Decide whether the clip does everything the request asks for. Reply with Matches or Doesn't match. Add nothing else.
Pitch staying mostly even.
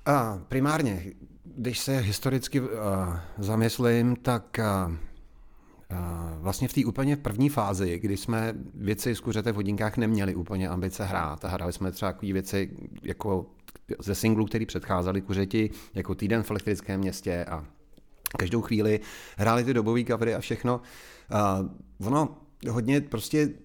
Doesn't match